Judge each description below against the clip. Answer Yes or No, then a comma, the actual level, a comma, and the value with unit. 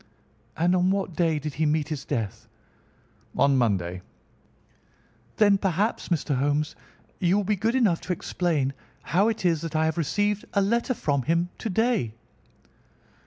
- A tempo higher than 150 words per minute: Yes, average, 160 wpm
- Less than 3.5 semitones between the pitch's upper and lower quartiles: No, wide, 5.4 semitones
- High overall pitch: No, medium, 170 Hz